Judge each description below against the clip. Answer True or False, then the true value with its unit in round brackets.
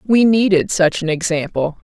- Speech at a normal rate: True (155 wpm)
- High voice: False (180 Hz)